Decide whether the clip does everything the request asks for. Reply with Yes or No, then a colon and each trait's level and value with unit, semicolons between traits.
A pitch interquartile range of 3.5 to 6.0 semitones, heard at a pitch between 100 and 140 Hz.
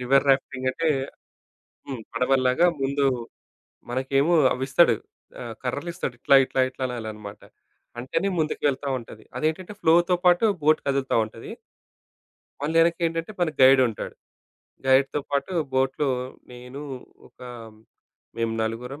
Yes: average, 3.9 semitones; low, 135 Hz